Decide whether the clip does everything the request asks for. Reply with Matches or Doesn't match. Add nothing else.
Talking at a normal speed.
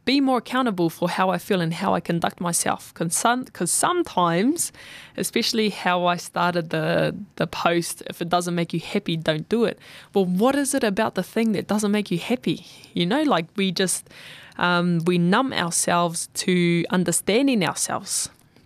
Matches